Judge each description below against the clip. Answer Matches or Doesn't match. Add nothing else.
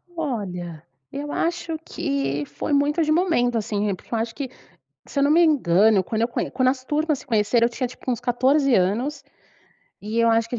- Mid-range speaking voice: Doesn't match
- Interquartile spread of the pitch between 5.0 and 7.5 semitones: Matches